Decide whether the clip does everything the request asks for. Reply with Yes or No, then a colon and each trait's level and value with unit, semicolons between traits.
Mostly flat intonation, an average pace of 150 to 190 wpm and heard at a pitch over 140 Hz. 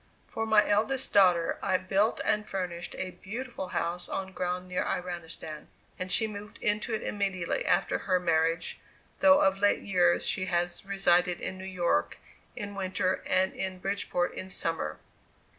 Yes: narrow, 2.3 semitones; average, 160 wpm; medium, 185 Hz